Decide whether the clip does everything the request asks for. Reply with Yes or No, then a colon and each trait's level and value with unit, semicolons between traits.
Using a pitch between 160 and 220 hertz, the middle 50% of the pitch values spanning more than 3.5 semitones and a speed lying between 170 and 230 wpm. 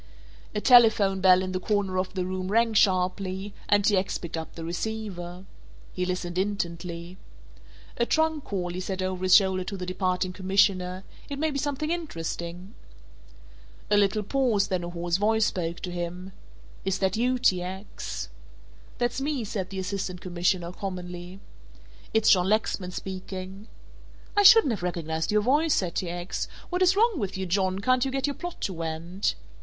No: high, 190 Hz; average, 3.2 semitones; average, 175 wpm